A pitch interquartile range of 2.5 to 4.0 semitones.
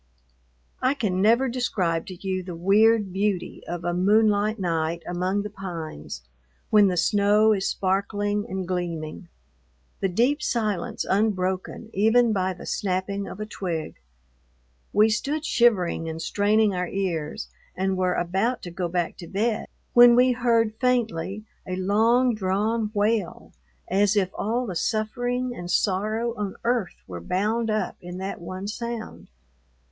Yes: average, 3.4 semitones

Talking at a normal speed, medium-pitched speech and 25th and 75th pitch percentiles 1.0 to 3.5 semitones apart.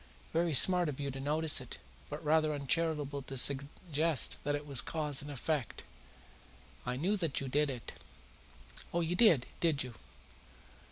Yes: average, 160 wpm; medium, 145 Hz; average, 2.8 semitones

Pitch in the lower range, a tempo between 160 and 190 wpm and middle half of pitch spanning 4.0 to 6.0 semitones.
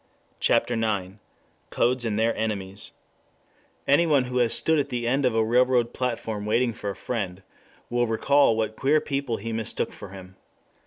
No: low, 115 Hz; average, 165 wpm; average, 2.9 semitones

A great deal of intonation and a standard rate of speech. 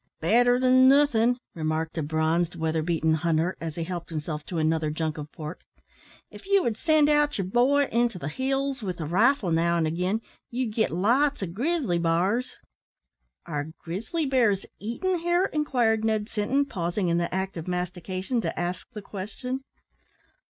Yes: wide, 7.2 semitones; average, 165 wpm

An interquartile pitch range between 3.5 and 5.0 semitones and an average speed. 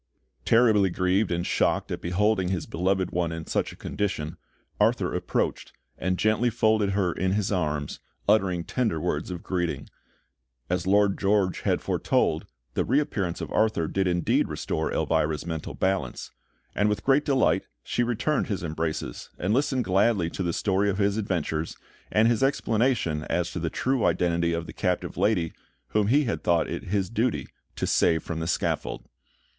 Yes: average, 4.0 semitones; average, 170 wpm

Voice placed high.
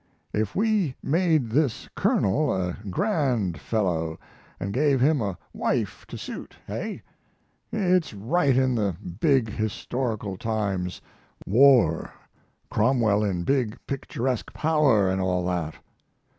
No: low, 115 Hz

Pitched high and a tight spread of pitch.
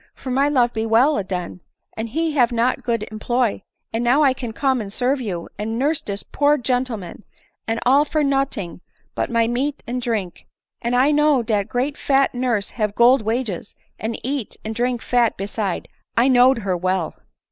No: high, 240 Hz; average, 3.4 semitones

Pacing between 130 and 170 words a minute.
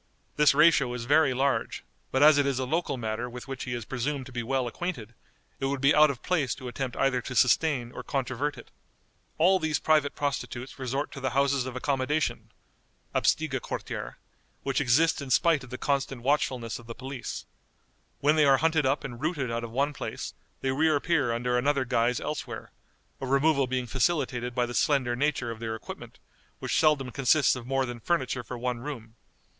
No: average, 195 wpm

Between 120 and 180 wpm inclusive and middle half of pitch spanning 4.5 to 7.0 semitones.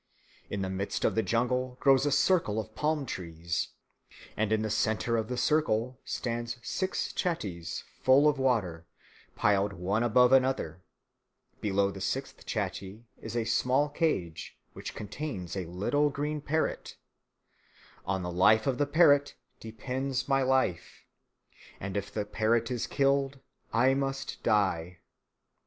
Yes: average, 145 wpm; average, 5.3 semitones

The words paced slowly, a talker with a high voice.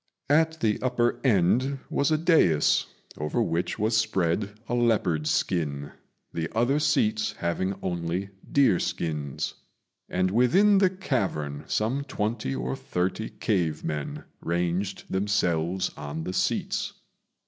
No: slow, 125 wpm; very low, 95 Hz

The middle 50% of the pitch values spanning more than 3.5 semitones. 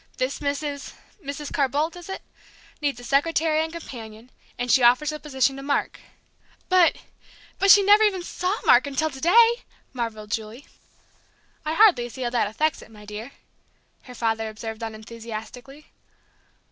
Yes: average, 5.3 semitones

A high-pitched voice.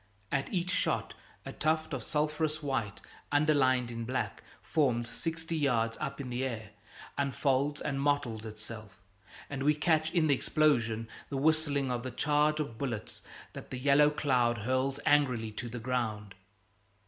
No: low, 135 Hz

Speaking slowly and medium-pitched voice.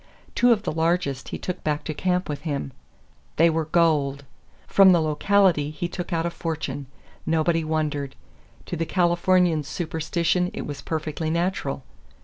No: average, 155 wpm; medium, 165 Hz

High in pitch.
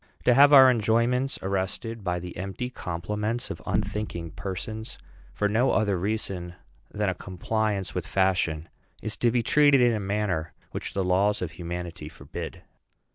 No: low, 100 Hz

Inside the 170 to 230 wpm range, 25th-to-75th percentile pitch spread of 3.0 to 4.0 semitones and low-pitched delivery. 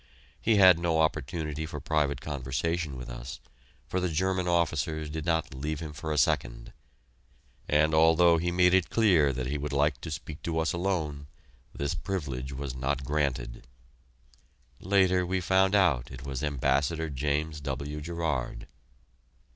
No: average, 155 wpm; average, 3.5 semitones; very low, 75 Hz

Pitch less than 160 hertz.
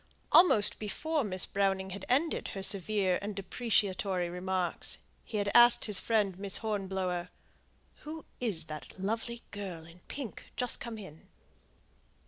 No: high, 200 Hz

